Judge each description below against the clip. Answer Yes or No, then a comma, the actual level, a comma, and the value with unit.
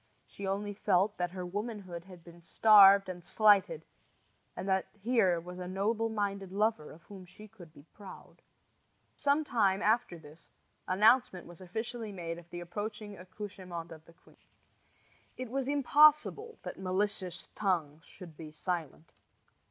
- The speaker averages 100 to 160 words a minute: Yes, average, 150 wpm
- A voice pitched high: Yes, high, 195 Hz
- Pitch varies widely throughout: No, average, 3.5 semitones